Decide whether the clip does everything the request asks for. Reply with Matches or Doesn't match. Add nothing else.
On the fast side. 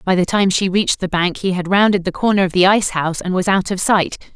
Matches